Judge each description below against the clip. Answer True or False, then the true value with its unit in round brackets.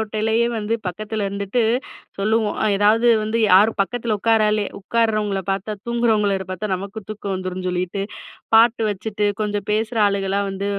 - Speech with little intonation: True (2.0 semitones)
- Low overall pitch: False (210 Hz)